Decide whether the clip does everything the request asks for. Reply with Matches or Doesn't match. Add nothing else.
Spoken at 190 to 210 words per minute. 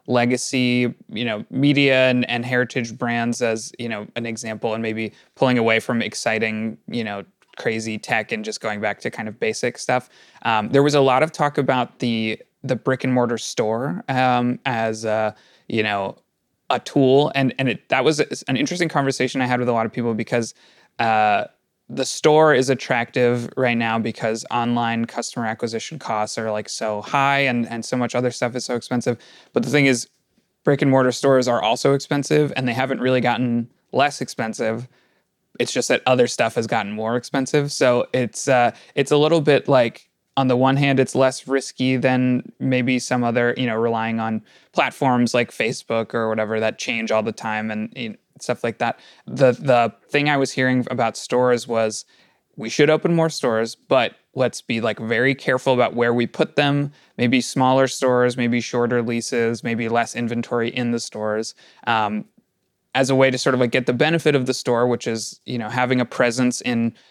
Matches